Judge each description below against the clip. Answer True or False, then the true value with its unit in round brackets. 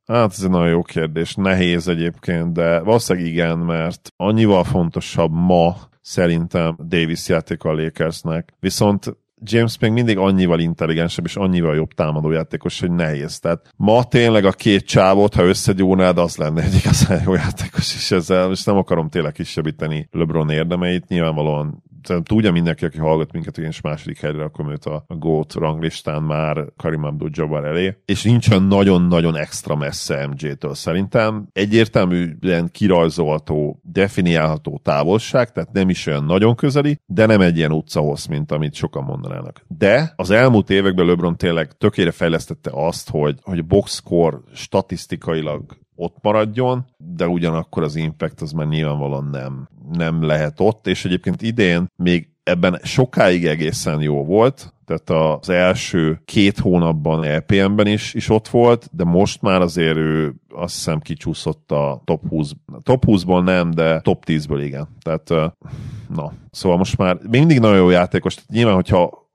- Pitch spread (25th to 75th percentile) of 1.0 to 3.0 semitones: False (3.8 semitones)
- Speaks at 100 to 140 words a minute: False (155 wpm)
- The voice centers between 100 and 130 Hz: False (85 Hz)